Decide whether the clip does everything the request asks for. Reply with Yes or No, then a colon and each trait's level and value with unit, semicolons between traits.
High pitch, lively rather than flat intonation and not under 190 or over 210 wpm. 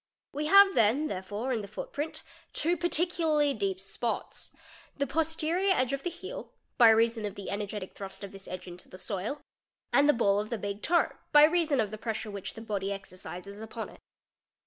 Yes: high, 230 Hz; wide, 7.4 semitones; fast, 205 wpm